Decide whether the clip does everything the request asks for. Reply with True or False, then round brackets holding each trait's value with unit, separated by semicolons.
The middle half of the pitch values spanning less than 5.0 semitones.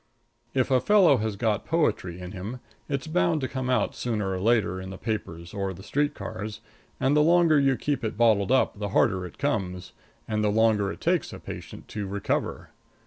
False (5.5 semitones)